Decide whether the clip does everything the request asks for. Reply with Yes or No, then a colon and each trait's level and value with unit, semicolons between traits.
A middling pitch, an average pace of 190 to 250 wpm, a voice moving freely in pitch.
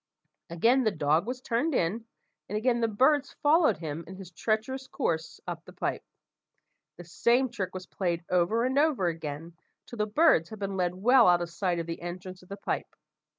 No: high, 195 Hz; average, 195 wpm; wide, 6.1 semitones